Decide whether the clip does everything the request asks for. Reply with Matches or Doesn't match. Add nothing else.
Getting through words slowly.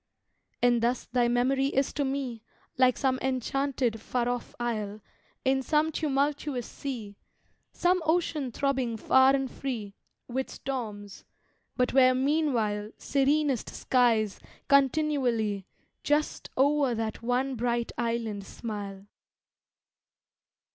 Matches